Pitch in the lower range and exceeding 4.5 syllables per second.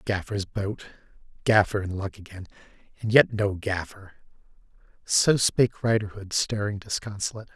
Yes: low, 105 Hz; 4.9 syllables/s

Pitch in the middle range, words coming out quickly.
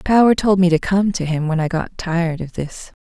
Yes: medium, 175 Hz; fast, 255 wpm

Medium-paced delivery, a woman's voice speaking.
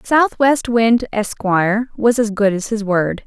Yes: average, 165 wpm; female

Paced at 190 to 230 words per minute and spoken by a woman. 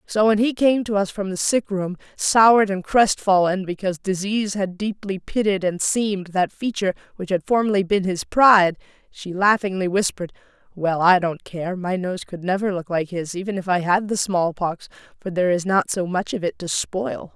Yes: average, 200 wpm; female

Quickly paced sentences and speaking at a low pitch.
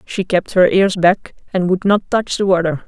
No: fast, 230 wpm; medium, 185 Hz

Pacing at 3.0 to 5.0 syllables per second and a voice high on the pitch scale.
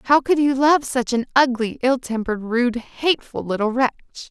No: 5.4 syllables/s; very high, 250 Hz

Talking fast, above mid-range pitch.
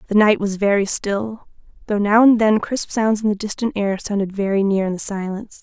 Yes: fast, 225 wpm; high, 205 Hz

